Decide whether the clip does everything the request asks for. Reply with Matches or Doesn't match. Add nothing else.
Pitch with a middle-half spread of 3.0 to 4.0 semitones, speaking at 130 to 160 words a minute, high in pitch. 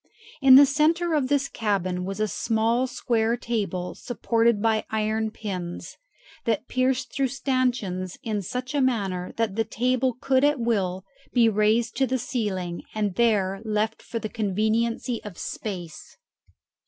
Matches